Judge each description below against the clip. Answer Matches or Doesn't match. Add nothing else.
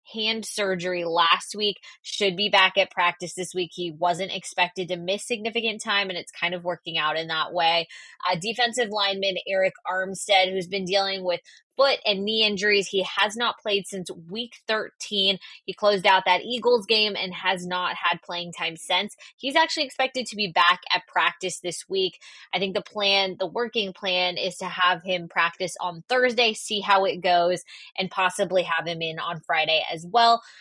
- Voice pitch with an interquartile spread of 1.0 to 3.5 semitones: Matches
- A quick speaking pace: Doesn't match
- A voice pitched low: Doesn't match